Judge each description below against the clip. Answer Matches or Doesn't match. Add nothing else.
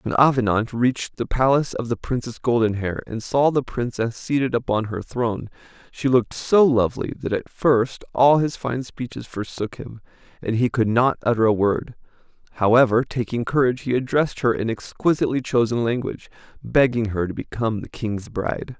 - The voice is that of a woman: Doesn't match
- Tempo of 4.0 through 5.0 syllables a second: Doesn't match